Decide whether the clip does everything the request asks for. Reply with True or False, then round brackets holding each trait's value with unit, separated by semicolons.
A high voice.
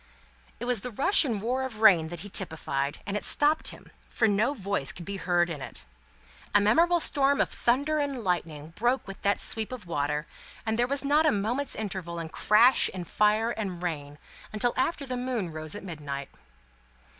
True (210 Hz)